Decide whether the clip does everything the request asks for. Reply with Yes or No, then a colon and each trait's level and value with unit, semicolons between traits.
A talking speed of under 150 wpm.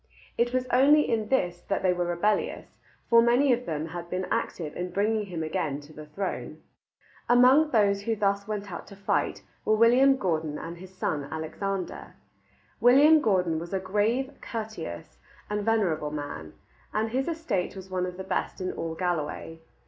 No: average, 175 wpm